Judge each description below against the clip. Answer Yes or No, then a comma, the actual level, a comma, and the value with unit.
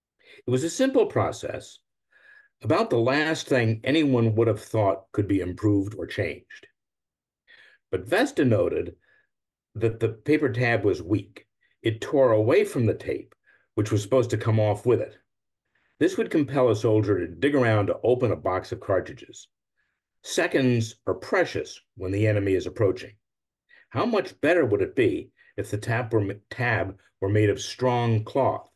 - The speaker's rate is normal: Yes, average, 160 wpm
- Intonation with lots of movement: No, average, 3.4 semitones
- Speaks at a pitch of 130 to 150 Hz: No, low, 115 Hz